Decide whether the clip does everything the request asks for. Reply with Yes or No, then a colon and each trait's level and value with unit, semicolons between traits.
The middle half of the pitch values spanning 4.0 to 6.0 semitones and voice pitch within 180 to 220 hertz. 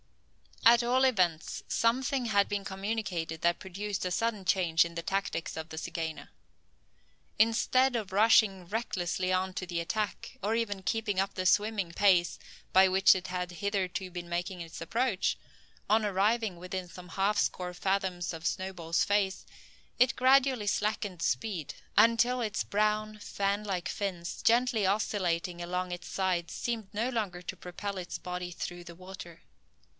No: average, 3.3 semitones; high, 190 Hz